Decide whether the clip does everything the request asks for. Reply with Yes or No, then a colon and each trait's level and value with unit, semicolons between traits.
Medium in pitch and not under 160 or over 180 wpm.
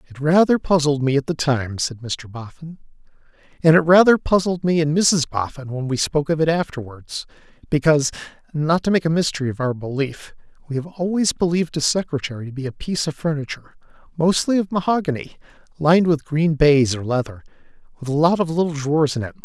No: medium, 150 Hz; average, 190 wpm